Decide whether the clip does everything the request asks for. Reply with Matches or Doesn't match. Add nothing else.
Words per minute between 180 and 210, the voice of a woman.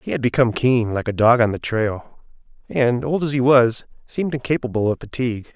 Doesn't match